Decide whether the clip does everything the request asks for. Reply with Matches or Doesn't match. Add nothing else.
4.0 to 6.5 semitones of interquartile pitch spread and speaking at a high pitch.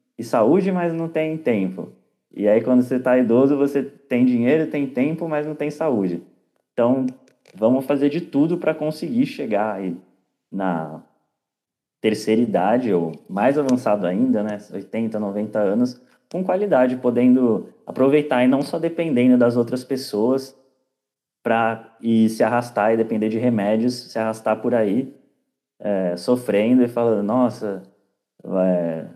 Doesn't match